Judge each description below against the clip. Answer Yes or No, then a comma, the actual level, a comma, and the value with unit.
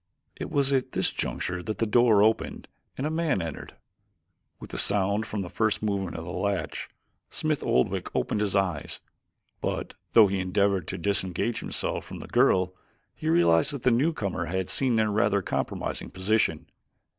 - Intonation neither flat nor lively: Yes, average, 3.6 semitones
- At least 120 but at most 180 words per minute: Yes, average, 170 wpm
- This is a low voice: Yes, low, 100 Hz